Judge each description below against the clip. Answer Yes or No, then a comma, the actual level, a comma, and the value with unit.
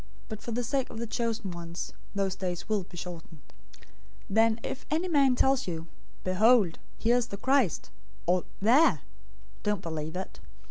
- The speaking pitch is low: No, high, 210 Hz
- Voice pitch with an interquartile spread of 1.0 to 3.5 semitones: No, wide, 5.6 semitones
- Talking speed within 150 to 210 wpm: Yes, average, 170 wpm